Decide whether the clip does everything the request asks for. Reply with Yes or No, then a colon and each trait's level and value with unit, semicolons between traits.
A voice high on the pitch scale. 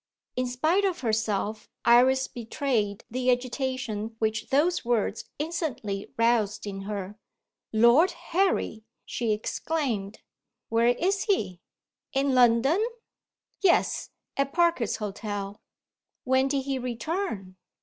Yes: high, 245 Hz